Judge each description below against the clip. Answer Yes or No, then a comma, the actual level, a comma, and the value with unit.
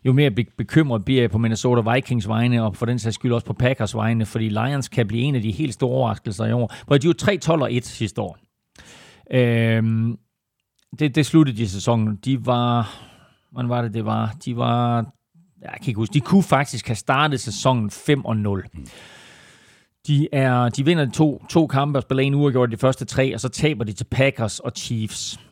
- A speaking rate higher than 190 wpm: Yes, average, 205 wpm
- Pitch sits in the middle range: No, low, 120 Hz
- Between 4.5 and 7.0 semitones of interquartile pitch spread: No, average, 3.2 semitones